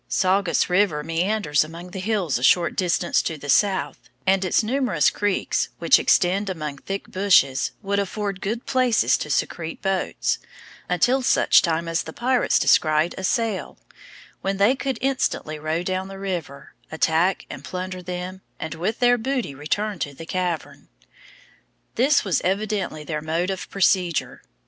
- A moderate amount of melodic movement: Yes, average, 4.0 semitones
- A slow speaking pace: No, average, 155 wpm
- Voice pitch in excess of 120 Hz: Yes, medium, 185 Hz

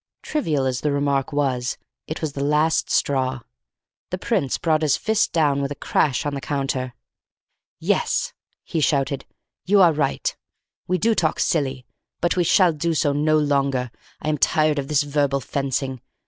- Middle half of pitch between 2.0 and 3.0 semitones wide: Yes, narrow, 2.4 semitones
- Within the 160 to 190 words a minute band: Yes, average, 170 wpm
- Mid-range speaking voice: Yes, medium, 145 Hz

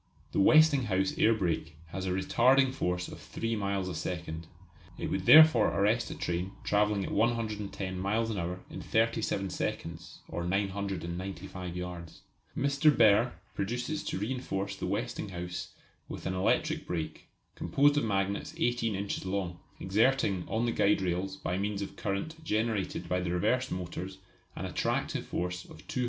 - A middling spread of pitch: Yes, average, 4.0 semitones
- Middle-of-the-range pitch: No, low, 100 Hz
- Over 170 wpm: No, average, 155 wpm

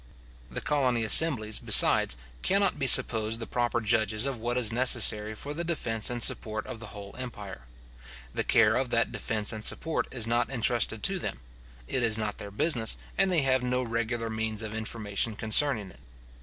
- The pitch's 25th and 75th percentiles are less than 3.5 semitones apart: Yes, average, 2.8 semitones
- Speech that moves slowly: No, average, 185 wpm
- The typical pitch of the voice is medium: No, low, 115 Hz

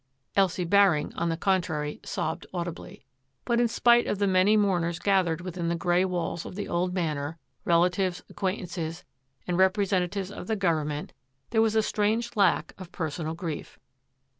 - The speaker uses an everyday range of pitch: Yes, average, 3.0 semitones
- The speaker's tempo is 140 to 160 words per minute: No, average, 170 wpm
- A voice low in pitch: No, medium, 180 Hz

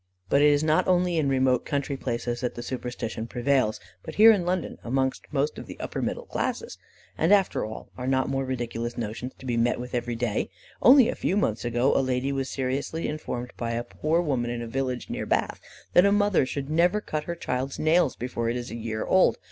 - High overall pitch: No, low, 130 Hz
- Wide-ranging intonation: No, average, 4.4 semitones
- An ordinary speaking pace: No, fast, 220 wpm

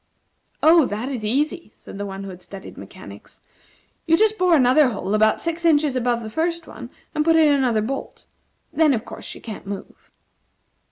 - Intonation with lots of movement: Yes, wide, 6.9 semitones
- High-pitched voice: Yes, very high, 265 Hz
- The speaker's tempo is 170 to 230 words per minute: Yes, average, 185 wpm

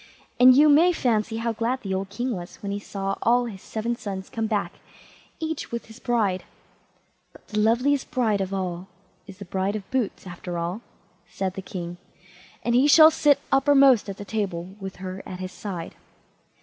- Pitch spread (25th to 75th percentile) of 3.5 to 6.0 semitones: Yes, average, 4.4 semitones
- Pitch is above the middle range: Yes, high, 210 Hz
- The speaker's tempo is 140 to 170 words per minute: No, average, 185 wpm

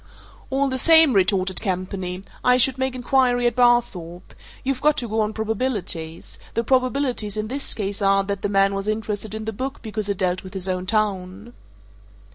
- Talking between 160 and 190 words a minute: Yes, average, 185 wpm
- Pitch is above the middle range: Yes, high, 215 Hz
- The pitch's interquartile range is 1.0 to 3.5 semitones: No, average, 4.4 semitones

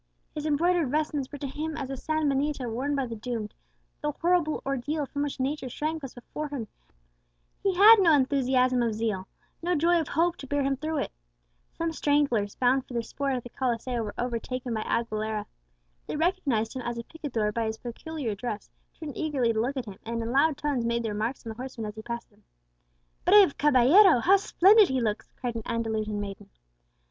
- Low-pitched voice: No, very high, 260 Hz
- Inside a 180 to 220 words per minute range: Yes, fast, 205 wpm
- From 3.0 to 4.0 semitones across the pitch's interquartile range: No, average, 4.6 semitones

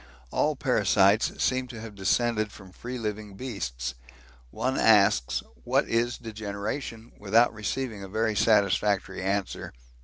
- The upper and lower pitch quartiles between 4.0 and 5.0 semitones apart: No, average, 2.9 semitones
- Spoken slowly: Yes, slow, 125 wpm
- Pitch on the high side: No, low, 105 Hz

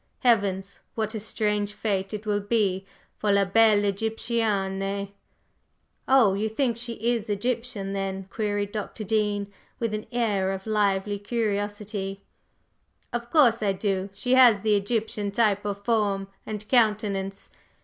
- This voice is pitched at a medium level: No, high, 210 Hz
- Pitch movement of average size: No, narrow, 2.0 semitones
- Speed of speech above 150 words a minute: No, average, 140 wpm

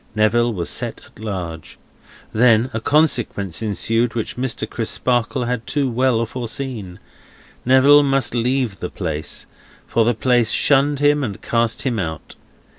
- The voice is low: Yes, low, 120 Hz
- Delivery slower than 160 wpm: Yes, average, 140 wpm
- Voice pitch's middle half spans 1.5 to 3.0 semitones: No, average, 3.4 semitones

